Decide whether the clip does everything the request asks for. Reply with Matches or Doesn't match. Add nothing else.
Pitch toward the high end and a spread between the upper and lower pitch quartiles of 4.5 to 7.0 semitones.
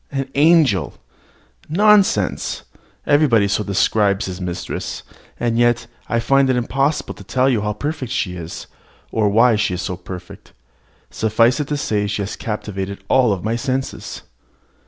Doesn't match